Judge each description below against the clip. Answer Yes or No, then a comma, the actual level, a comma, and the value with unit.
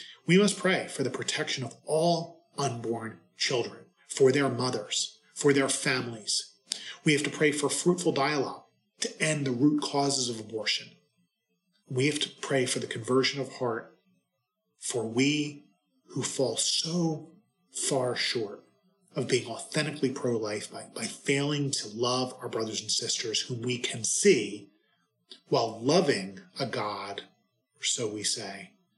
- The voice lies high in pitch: No, medium, 140 Hz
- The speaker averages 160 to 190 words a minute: No, average, 150 wpm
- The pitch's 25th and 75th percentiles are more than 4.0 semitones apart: Yes, average, 4.8 semitones